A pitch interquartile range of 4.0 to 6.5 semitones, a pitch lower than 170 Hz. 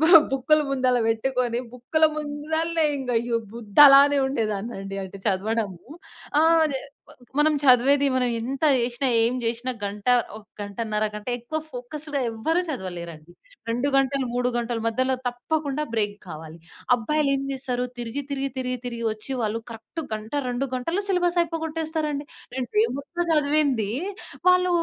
No: average, 4.5 semitones; very high, 255 Hz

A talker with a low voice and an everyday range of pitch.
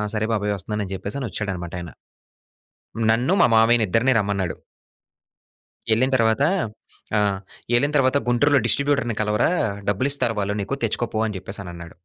Yes: low, 110 Hz; average, 3.7 semitones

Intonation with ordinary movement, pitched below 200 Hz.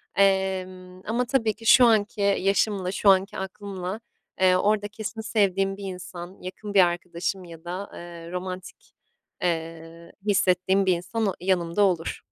No: narrow, 2.1 semitones; high, 190 Hz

